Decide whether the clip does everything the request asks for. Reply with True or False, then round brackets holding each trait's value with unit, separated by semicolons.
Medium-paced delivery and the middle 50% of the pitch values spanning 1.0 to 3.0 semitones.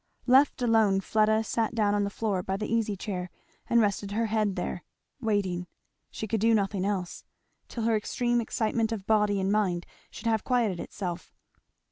True (175 wpm; 2.5 semitones)